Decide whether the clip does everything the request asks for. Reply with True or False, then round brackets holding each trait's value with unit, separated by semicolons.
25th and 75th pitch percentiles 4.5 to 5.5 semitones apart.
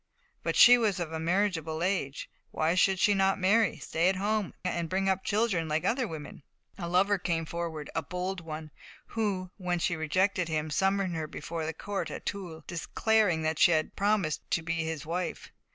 False (3.3 semitones)